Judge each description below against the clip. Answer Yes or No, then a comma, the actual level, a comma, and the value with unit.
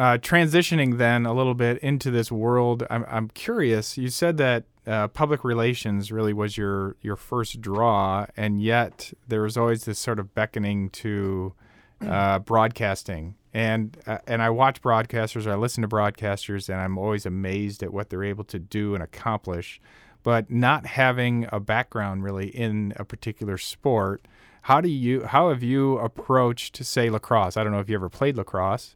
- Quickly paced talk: No, average, 180 wpm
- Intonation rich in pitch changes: No, average, 3.1 semitones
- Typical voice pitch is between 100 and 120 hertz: Yes, low, 110 Hz